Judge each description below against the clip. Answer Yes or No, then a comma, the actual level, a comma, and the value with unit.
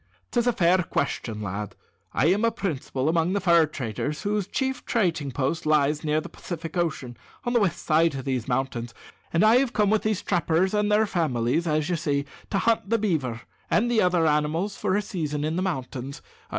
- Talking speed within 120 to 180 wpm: No, average, 200 wpm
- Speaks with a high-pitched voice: No, medium, 165 Hz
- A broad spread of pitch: Yes, wide, 5.9 semitones